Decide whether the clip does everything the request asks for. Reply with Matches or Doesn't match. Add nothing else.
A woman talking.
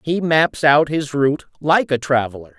Doesn't match